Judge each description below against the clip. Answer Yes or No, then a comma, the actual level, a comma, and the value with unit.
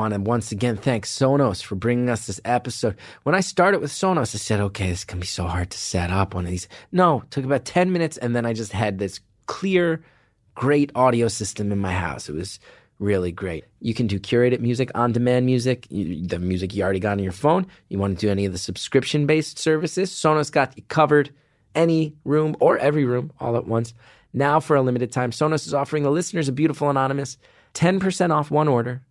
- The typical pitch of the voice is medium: No, low, 125 Hz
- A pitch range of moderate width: No, wide, 6.6 semitones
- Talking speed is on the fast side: Yes, fast, 220 wpm